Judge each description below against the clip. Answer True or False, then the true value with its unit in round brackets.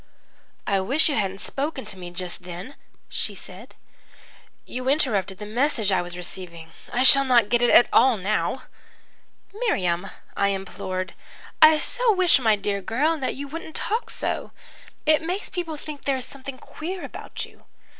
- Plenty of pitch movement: True (7.8 semitones)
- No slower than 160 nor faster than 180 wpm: True (165 wpm)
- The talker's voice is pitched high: True (245 Hz)